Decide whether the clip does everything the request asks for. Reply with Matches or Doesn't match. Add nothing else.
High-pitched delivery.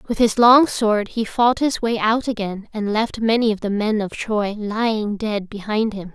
Matches